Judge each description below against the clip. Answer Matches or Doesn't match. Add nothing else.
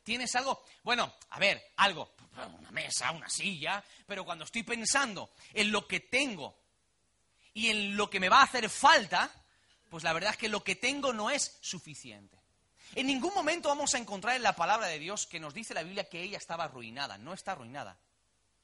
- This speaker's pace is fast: Matches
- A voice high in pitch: Matches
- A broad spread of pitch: Matches